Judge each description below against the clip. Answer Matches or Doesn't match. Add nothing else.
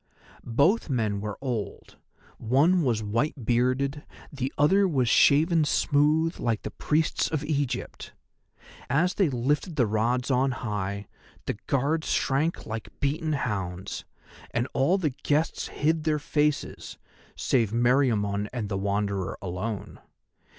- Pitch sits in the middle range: Doesn't match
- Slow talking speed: Matches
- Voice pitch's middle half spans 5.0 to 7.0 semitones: Matches